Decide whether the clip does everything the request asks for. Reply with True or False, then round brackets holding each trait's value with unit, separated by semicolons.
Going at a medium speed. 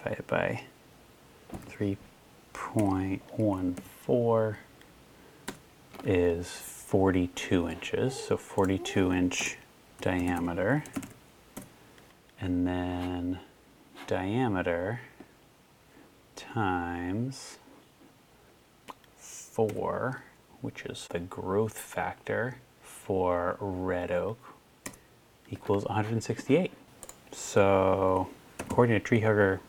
False (60 wpm)